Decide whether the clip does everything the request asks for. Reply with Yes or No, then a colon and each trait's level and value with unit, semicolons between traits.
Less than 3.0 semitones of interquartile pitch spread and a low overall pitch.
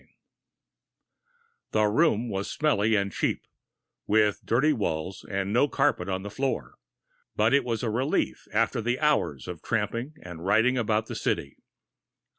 No: average, 4.0 semitones; low, 110 Hz